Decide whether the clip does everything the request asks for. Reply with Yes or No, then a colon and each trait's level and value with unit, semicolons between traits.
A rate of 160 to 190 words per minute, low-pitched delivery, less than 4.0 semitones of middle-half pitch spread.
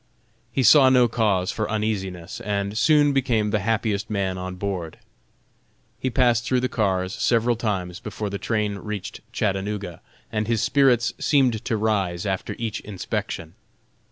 No: average, 150 wpm; low, 105 Hz; average, 3.4 semitones